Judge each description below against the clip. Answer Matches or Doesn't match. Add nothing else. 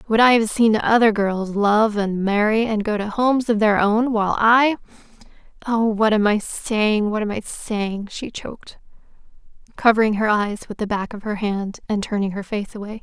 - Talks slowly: Doesn't match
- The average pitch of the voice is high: Matches